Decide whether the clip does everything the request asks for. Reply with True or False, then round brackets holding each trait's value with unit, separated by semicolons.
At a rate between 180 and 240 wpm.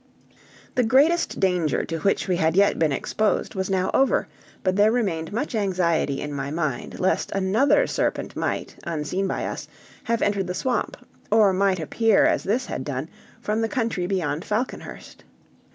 False (170 wpm)